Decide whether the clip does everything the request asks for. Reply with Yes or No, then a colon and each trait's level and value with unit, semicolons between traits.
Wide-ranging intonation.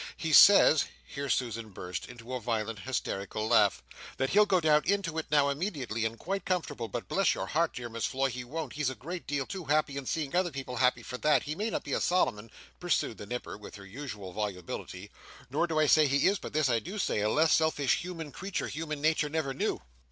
Yes: wide, 5.7 semitones